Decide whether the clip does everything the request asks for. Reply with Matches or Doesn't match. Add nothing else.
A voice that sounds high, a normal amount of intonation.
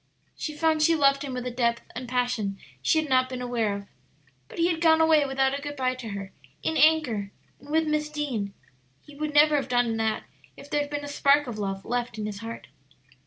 Matches